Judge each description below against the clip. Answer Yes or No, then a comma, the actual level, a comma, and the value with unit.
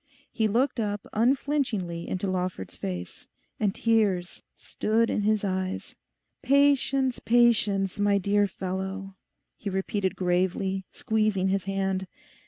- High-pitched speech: Yes, high, 200 Hz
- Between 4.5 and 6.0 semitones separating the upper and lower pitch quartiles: No, average, 2.8 semitones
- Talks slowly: Yes, slow, 115 wpm